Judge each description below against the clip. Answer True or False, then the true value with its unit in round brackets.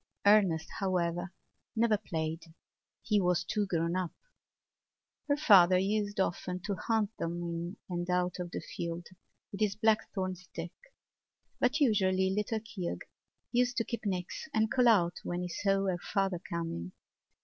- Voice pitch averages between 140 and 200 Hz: True (185 Hz)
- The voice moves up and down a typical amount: True (3.5 semitones)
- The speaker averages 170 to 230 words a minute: False (145 wpm)